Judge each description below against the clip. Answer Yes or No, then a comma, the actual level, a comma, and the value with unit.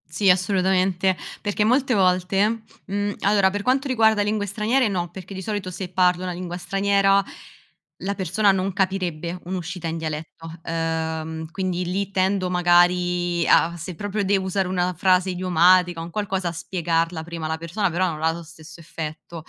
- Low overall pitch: No, medium, 185 Hz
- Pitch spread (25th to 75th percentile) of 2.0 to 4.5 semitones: Yes, narrow, 2.4 semitones